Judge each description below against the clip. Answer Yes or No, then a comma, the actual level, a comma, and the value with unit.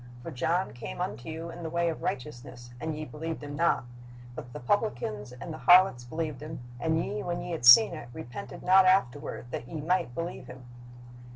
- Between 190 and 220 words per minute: Yes, average, 200 wpm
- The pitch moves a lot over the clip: Yes, wide, 5.7 semitones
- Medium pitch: Yes, medium, 155 Hz